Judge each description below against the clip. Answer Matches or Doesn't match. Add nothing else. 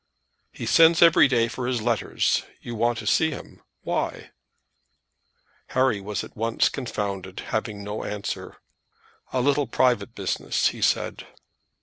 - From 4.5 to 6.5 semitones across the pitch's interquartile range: Doesn't match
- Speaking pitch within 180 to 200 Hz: Doesn't match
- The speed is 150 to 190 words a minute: Doesn't match